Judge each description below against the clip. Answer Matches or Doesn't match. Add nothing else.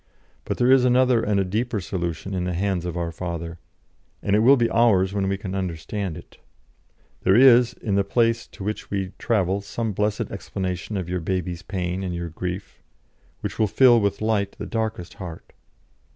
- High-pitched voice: Doesn't match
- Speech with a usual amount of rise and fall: Matches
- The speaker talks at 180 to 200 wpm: Matches